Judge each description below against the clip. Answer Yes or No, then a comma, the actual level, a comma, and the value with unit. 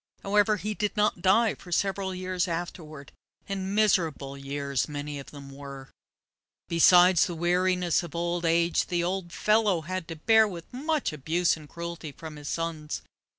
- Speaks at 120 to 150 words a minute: No, average, 160 wpm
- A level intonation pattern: No, average, 3.7 semitones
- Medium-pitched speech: Yes, medium, 175 Hz